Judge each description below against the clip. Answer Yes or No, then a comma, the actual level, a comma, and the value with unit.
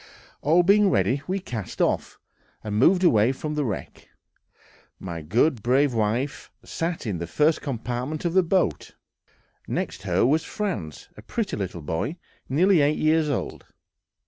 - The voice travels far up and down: Yes, wide, 7.3 semitones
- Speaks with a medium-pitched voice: Yes, medium, 145 Hz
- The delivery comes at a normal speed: Yes, average, 150 wpm